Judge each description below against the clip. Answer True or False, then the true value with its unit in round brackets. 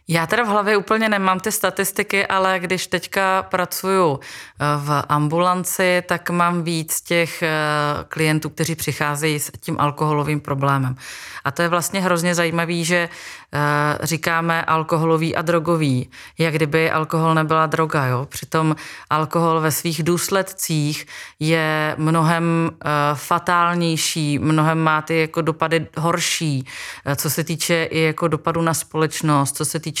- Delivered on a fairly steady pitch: True (2.1 semitones)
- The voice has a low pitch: False (160 Hz)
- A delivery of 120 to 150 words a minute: True (135 wpm)